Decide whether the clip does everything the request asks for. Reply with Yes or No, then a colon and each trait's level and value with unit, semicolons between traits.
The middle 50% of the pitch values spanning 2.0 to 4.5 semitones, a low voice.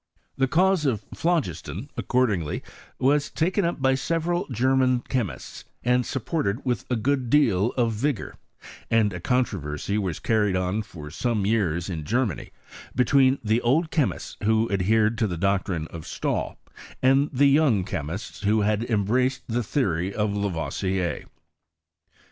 No: average, 5.2 semitones; low, 115 Hz